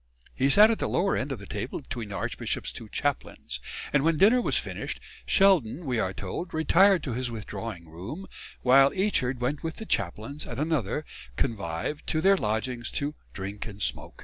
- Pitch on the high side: No, low, 135 Hz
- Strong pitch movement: Yes, wide, 7.0 semitones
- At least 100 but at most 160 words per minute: No, average, 185 wpm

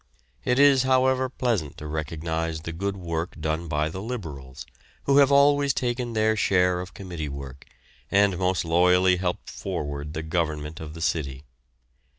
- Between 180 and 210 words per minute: No, average, 160 wpm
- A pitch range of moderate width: No, wide, 5.9 semitones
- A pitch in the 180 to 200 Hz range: No, very low, 90 Hz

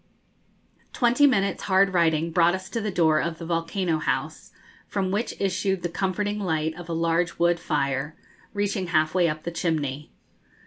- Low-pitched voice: No, medium, 175 Hz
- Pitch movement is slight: No, average, 3.2 semitones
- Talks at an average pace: Yes, average, 165 wpm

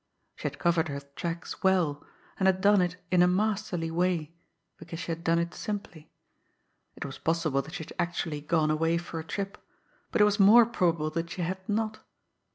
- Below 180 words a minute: No, average, 195 wpm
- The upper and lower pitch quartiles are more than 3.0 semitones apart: No, average, 2.7 semitones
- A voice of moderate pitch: Yes, medium, 170 Hz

